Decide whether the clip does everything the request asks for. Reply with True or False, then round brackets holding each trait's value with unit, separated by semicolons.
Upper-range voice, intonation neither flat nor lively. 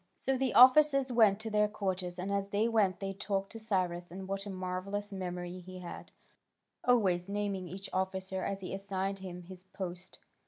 False (195 Hz; 2.0 semitones)